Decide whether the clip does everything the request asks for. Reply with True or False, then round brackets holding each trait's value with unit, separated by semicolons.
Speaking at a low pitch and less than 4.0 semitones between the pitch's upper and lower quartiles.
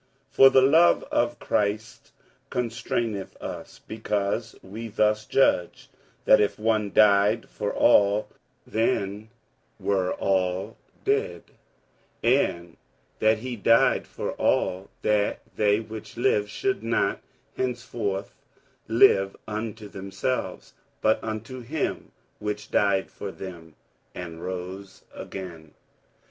True (105 Hz; 2.9 semitones)